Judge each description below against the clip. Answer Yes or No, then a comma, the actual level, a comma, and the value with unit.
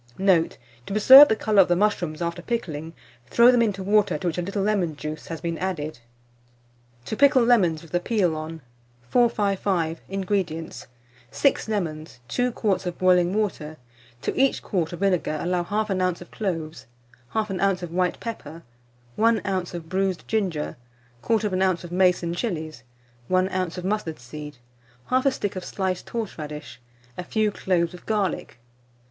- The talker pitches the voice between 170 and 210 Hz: Yes, medium, 185 Hz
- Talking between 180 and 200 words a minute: No, average, 165 wpm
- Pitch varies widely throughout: No, average, 3.9 semitones